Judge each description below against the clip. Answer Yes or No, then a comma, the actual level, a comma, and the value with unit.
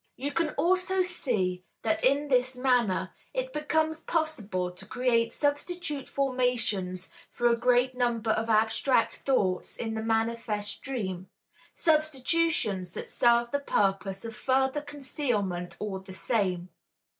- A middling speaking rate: No, slow, 130 wpm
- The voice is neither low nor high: No, high, 240 Hz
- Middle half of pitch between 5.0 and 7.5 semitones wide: Yes, wide, 5.6 semitones